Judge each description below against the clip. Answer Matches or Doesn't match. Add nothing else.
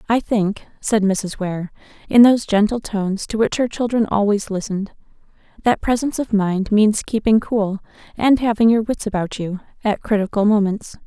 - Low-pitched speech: Doesn't match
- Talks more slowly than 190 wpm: Matches